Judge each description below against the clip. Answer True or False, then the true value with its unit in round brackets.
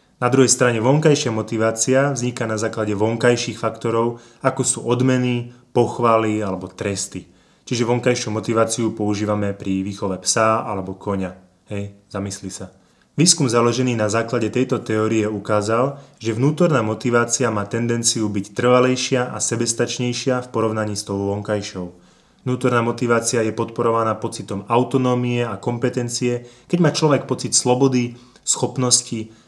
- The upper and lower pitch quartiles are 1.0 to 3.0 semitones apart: True (2.4 semitones)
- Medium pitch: False (115 Hz)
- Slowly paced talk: False (130 wpm)